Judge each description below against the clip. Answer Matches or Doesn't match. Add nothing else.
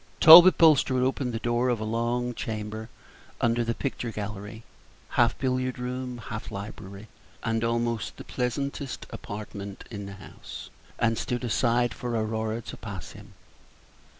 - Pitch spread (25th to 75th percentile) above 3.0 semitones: Doesn't match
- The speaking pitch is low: Matches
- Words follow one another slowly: Doesn't match